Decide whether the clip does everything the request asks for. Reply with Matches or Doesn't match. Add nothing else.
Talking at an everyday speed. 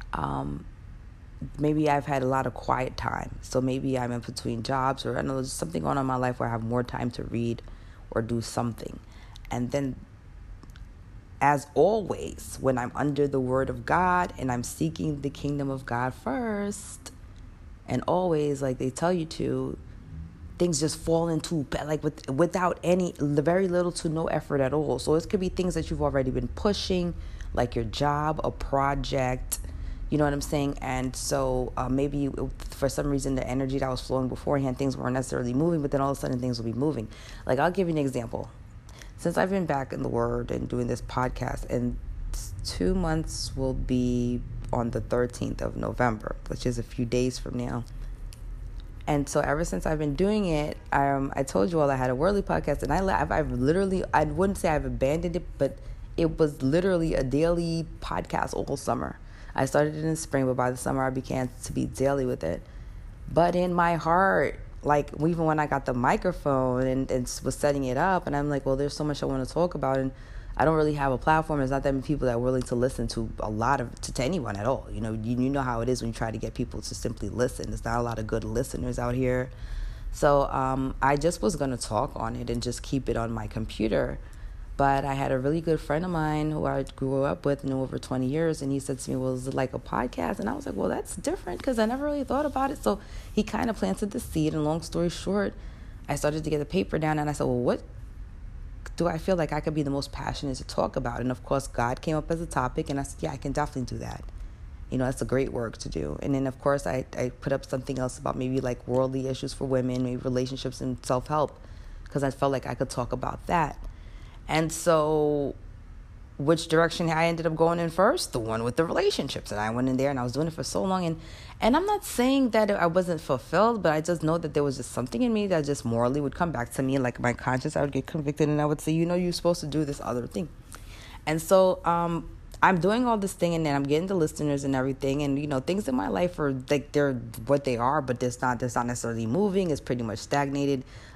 Doesn't match